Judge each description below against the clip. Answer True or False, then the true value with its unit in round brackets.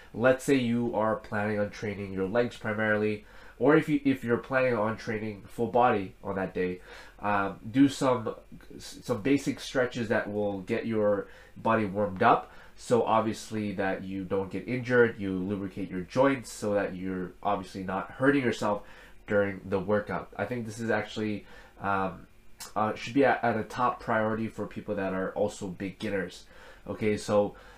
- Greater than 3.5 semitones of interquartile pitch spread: False (3.1 semitones)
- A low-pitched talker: True (105 Hz)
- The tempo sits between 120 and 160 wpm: False (170 wpm)